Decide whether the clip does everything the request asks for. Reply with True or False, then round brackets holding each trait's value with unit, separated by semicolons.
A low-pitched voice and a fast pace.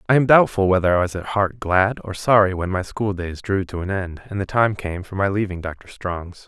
True (95 Hz; 260 wpm)